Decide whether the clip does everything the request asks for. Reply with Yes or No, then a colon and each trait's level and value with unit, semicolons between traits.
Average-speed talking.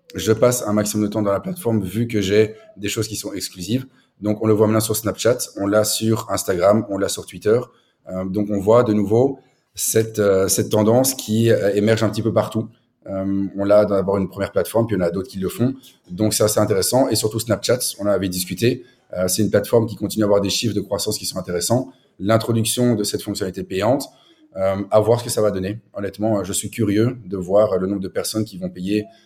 No: fast, 240 wpm